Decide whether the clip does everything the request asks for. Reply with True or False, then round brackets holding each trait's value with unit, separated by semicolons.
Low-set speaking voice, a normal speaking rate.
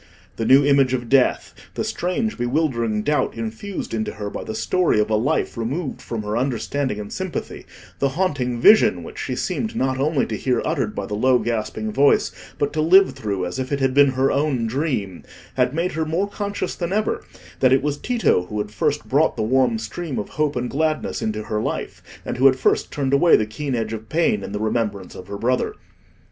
False (130 Hz; 215 wpm)